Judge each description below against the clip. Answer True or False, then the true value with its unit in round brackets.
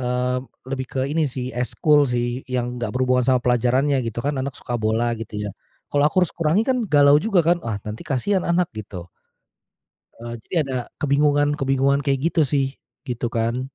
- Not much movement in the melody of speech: False (3.3 semitones)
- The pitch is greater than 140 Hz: False (130 Hz)